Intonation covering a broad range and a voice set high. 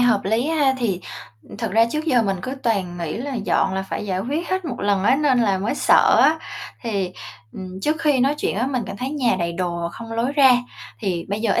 Yes: wide, 5.7 semitones; high, 230 Hz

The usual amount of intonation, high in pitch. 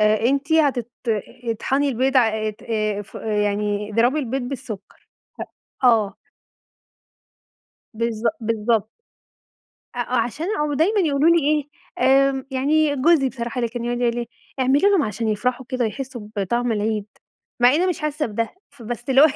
Yes: average, 3.8 semitones; high, 245 Hz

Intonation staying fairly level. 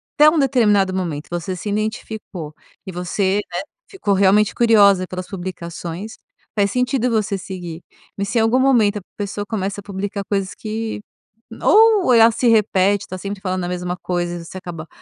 No: average, 3.2 semitones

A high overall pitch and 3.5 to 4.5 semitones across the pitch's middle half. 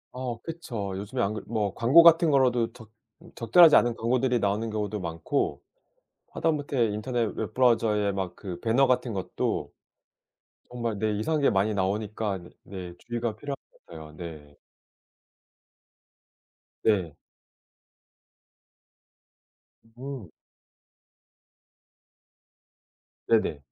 No: low, 110 Hz; average, 4.1 semitones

